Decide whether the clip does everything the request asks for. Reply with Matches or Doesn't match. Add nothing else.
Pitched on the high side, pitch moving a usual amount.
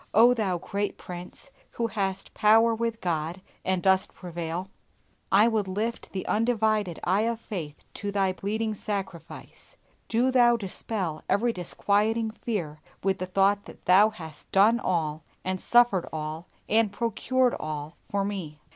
Matches